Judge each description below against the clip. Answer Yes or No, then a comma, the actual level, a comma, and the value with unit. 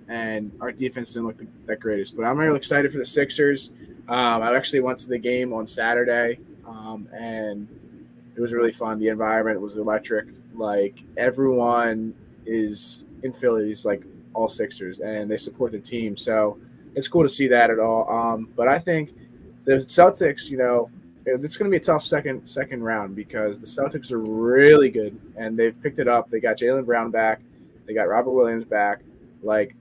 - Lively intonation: No, average, 2.9 semitones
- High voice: No, low, 115 Hz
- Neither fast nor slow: Yes, average, 185 wpm